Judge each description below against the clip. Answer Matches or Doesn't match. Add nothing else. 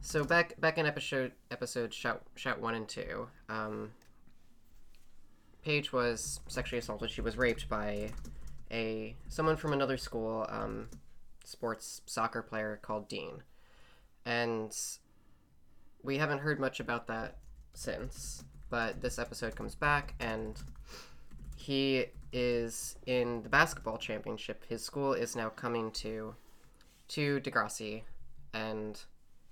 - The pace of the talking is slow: Matches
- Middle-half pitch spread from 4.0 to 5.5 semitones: Doesn't match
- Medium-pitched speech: Doesn't match